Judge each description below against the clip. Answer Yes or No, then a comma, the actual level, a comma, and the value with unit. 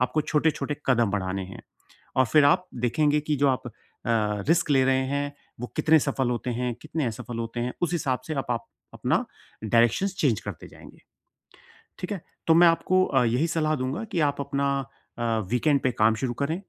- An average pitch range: Yes, average, 4.2 semitones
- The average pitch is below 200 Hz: Yes, medium, 140 Hz